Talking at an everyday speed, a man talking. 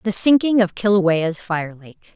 No: average, 165 wpm; female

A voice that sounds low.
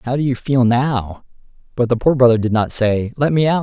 Yes: low, 125 Hz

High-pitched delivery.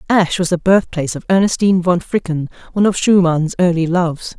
No: medium, 180 Hz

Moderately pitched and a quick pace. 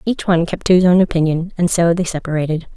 Yes: medium, 170 Hz; fast, 240 wpm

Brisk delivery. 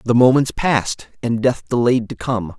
No: average, 185 wpm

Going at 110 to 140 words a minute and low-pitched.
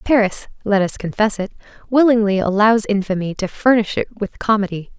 No: slow, 135 wpm; high, 210 Hz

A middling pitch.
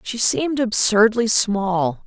No: high, 215 Hz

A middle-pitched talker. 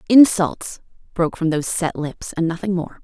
Yes: medium, 180 Hz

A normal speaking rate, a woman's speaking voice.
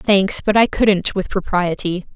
Yes: average, 165 wpm; female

